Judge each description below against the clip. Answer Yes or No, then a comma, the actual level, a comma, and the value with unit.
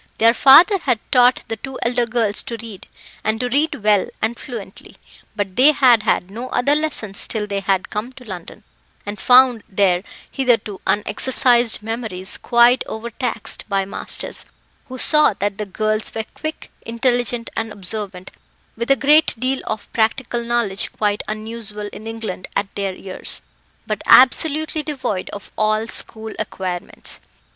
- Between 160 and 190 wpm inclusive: No, average, 150 wpm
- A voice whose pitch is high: Yes, high, 225 Hz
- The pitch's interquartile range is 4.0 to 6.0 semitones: No, average, 3.3 semitones